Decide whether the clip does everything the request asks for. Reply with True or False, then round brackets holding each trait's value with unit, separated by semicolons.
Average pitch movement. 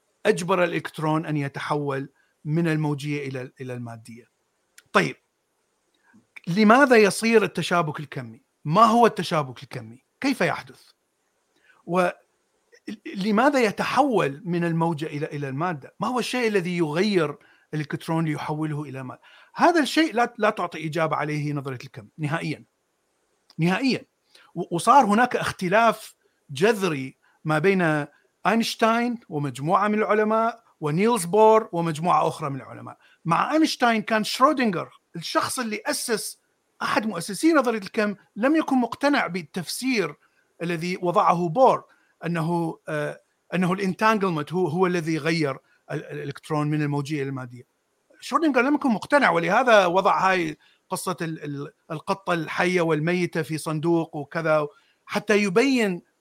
False (6.4 semitones)